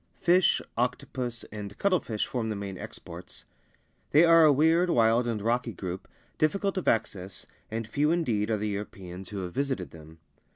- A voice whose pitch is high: No, low, 115 Hz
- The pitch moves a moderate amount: No, wide, 7.0 semitones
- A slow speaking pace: No, average, 165 wpm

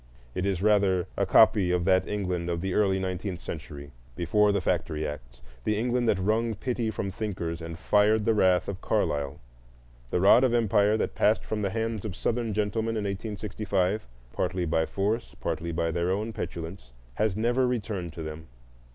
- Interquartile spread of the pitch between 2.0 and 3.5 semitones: No, average, 3.9 semitones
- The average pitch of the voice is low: Yes, very low, 95 Hz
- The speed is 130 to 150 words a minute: No, average, 175 wpm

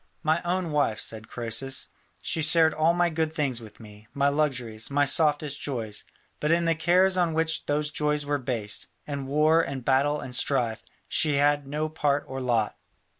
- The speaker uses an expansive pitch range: No, average, 3.5 semitones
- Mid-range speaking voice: Yes, medium, 145 Hz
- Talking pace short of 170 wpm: No, average, 180 wpm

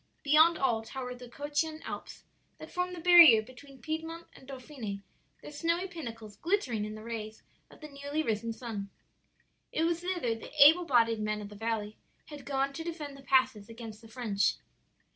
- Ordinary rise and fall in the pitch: No, wide, 5.8 semitones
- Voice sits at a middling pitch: No, very high, 260 Hz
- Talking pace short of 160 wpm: No, average, 180 wpm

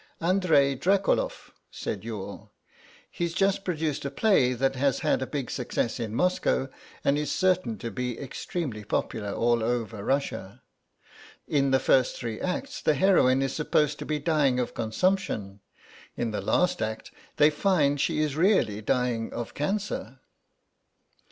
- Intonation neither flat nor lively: No, wide, 6.3 semitones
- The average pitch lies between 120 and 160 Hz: Yes, medium, 140 Hz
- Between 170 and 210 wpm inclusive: No, average, 150 wpm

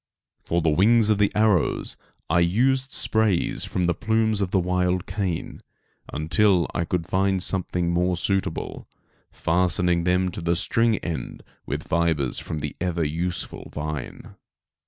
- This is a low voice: Yes, very low, 90 Hz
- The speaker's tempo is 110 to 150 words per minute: Yes, average, 145 wpm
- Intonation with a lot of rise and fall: No, average, 2.9 semitones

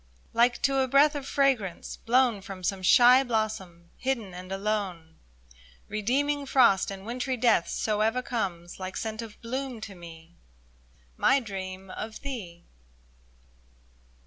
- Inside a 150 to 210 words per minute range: No, slow, 135 wpm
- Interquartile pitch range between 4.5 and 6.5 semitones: Yes, average, 5.1 semitones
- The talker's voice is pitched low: No, high, 220 Hz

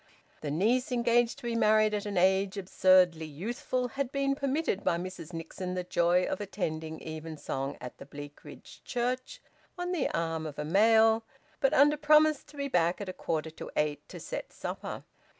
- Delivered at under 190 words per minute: Yes, average, 180 wpm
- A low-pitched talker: No, high, 195 Hz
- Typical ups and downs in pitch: No, wide, 7.3 semitones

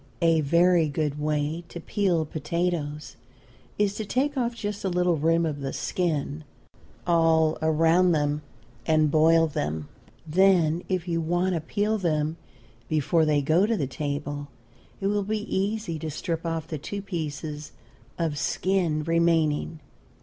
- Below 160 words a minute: Yes, average, 150 wpm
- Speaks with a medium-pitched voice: Yes, medium, 165 Hz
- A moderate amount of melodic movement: Yes, average, 3.0 semitones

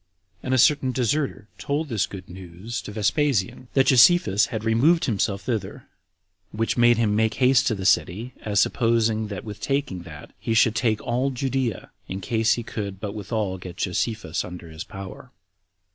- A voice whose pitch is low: Yes, low, 110 Hz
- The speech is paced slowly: No, average, 175 wpm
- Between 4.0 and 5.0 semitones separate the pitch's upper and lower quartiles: Yes, average, 4.4 semitones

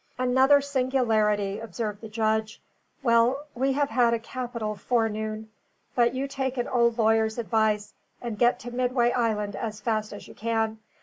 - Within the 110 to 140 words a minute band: No, average, 160 wpm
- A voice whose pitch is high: Yes, high, 230 Hz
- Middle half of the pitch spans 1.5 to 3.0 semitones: Yes, narrow, 2.5 semitones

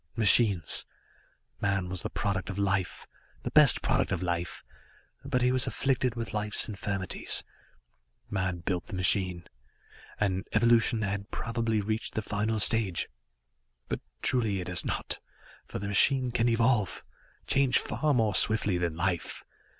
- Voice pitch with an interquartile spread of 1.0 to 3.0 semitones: No, average, 3.6 semitones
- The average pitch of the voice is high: No, low, 105 Hz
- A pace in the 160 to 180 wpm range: No, average, 140 wpm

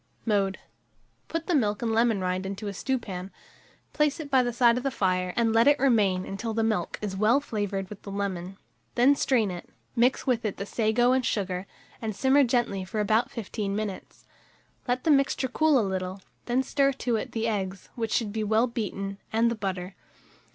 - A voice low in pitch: No, high, 220 Hz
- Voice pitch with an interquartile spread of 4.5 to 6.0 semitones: No, average, 4.0 semitones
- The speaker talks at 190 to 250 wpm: Yes, average, 200 wpm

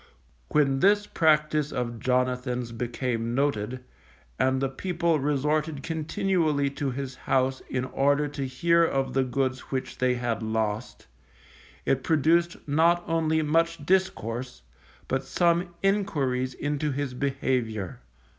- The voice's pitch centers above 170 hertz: No, low, 135 Hz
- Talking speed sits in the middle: No, slow, 125 wpm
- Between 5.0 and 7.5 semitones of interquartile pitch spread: No, average, 3.8 semitones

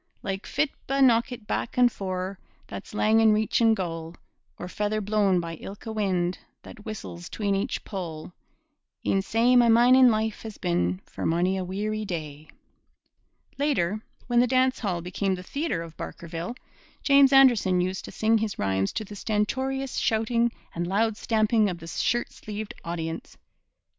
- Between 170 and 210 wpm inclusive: No, average, 160 wpm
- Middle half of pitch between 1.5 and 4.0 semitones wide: No, average, 4.4 semitones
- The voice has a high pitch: Yes, high, 210 Hz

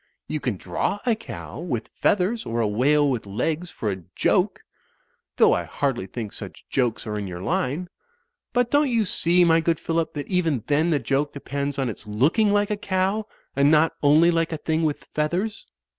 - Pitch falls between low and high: Yes, medium, 155 Hz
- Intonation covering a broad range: Yes, wide, 5.9 semitones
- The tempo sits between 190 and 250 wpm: Yes, fast, 205 wpm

